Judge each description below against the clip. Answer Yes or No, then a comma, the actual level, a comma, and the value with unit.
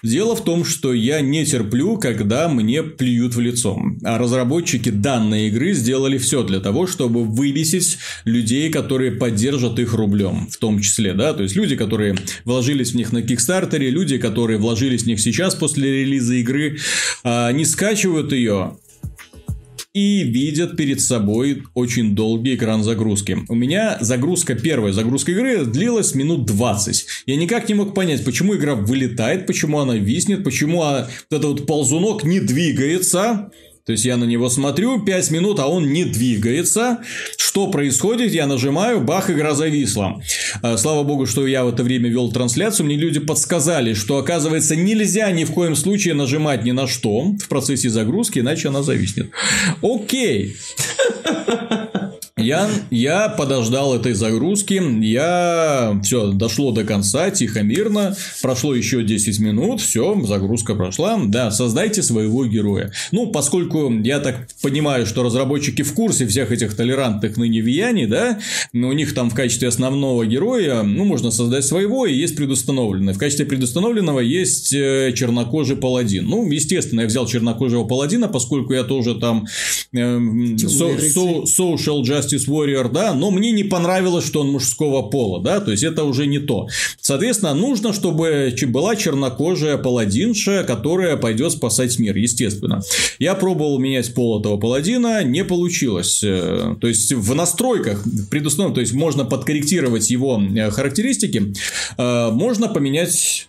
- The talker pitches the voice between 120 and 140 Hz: Yes, low, 135 Hz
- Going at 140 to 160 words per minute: Yes, average, 150 wpm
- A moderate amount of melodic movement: No, wide, 6.2 semitones